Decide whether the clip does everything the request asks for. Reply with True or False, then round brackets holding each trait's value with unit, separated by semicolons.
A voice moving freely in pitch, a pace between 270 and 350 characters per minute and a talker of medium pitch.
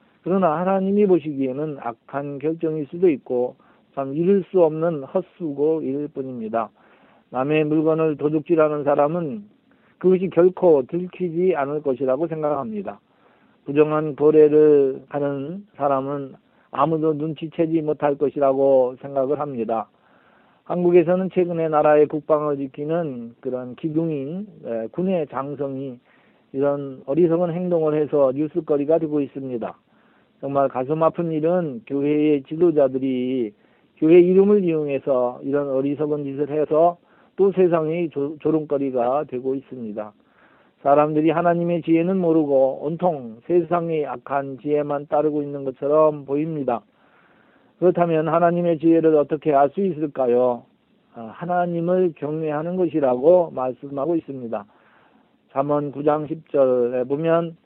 False (3.5 semitones; 290 characters per minute; 150 Hz)